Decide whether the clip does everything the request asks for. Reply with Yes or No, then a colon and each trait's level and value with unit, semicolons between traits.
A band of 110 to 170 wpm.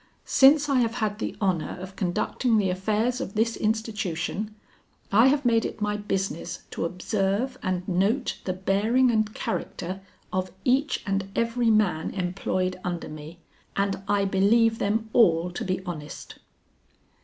Yes: average, 150 wpm